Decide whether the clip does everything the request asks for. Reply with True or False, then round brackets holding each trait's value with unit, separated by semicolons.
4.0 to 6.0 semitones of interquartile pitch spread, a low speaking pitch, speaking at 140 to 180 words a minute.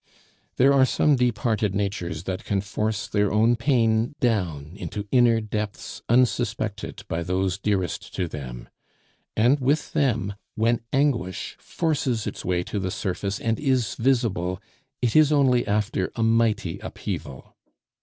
True (4.3 semitones; 110 Hz; 145 wpm)